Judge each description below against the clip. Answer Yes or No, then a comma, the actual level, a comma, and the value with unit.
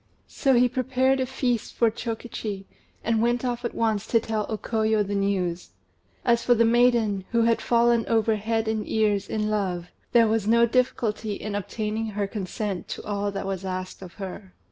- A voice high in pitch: Yes, high, 220 Hz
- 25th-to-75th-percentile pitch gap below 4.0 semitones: Yes, narrow, 2.6 semitones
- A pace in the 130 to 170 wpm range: No, average, 190 wpm